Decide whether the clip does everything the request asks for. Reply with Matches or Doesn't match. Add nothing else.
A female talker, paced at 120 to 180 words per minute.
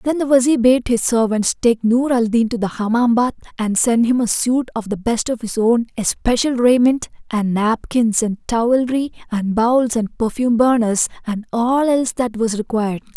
Doesn't match